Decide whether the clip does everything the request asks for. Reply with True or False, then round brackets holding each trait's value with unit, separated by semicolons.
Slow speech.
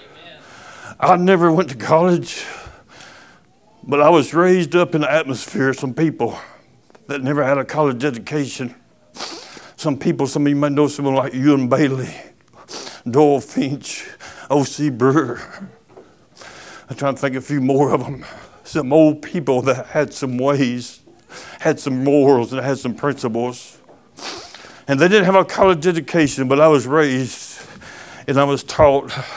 False (155 wpm)